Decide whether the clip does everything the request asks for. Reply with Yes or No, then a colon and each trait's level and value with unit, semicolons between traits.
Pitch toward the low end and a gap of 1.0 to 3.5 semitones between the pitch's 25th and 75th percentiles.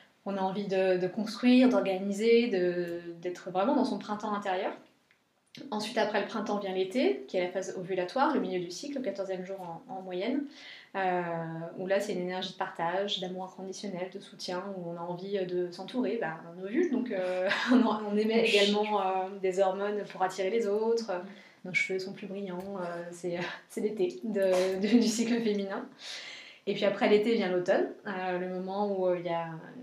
No: high, 195 Hz; narrow, 2.4 semitones